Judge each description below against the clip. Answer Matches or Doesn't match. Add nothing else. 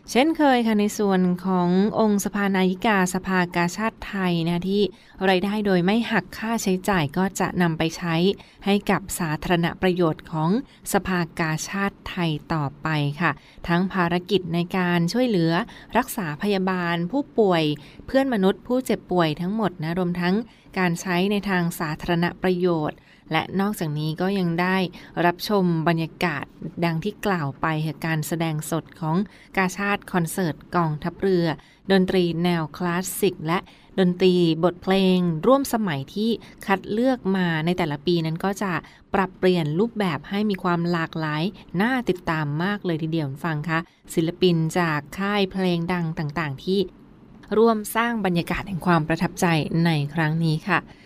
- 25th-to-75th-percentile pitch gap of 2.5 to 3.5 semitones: Matches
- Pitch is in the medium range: Matches